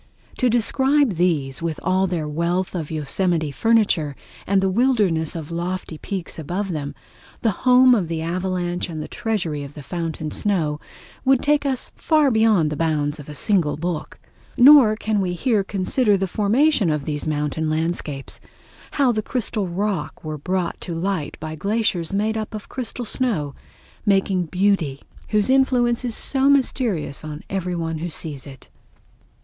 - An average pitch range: No, wide, 5.8 semitones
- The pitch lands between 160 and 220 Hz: Yes, medium, 185 Hz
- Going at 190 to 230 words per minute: No, average, 160 wpm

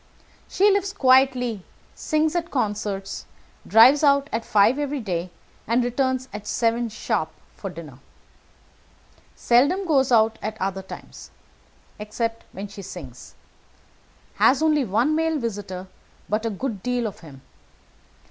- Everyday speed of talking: No, slow, 130 wpm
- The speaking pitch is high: Yes, high, 230 Hz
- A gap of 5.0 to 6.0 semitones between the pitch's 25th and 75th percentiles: Yes, average, 5.3 semitones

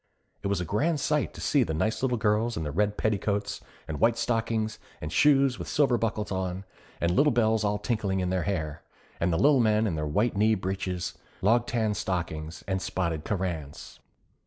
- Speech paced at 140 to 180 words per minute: No, average, 190 wpm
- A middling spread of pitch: Yes, average, 4.2 semitones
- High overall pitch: No, low, 105 Hz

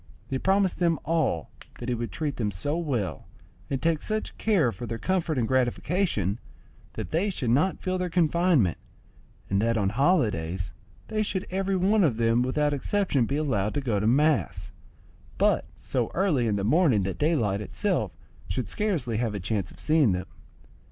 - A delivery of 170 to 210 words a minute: Yes, average, 180 wpm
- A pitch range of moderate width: No, wide, 7.7 semitones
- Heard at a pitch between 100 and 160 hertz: Yes, low, 135 Hz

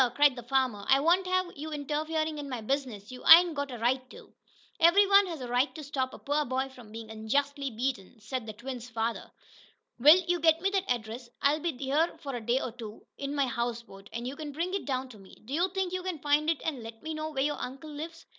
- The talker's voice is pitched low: No, very high, 275 Hz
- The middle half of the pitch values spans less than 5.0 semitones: Yes, average, 4.6 semitones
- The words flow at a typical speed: No, fast, 240 wpm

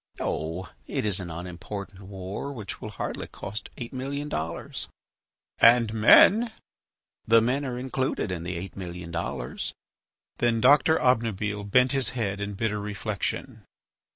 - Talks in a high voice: No, low, 105 Hz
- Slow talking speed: No, average, 145 wpm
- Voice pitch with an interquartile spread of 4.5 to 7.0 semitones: Yes, average, 4.9 semitones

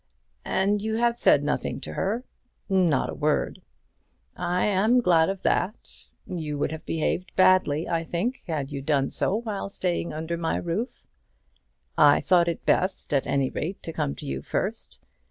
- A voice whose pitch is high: No, medium, 170 Hz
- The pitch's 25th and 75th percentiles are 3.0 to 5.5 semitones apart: Yes, average, 4.4 semitones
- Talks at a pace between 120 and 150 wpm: No, average, 170 wpm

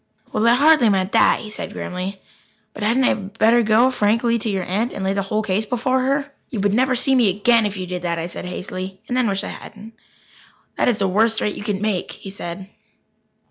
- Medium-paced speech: No, fast, 230 wpm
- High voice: Yes, high, 210 Hz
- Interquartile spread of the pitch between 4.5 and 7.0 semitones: No, average, 3.5 semitones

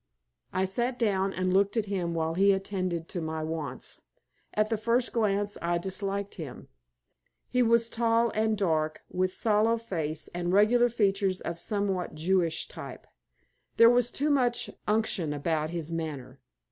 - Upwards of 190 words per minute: No, average, 155 wpm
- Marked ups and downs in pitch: No, average, 4.8 semitones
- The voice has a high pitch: Yes, high, 195 Hz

